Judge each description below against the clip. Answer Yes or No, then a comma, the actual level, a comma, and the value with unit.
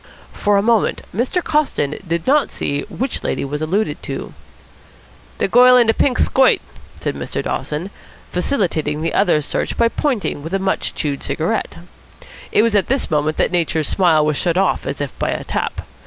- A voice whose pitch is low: No, medium, 185 Hz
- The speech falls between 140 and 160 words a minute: No, average, 185 wpm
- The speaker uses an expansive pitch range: Yes, wide, 7.2 semitones